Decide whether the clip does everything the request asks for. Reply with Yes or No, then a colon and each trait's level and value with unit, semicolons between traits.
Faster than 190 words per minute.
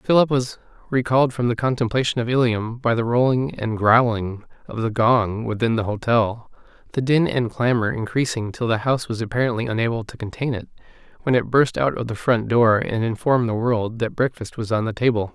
Yes: average, 200 wpm